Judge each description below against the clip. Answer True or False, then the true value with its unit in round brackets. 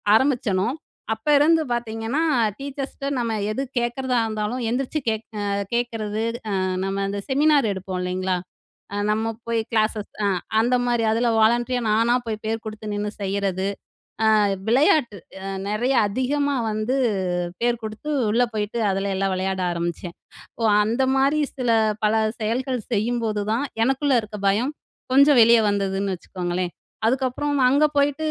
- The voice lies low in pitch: False (225 Hz)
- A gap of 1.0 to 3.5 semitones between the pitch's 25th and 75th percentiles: False (3.9 semitones)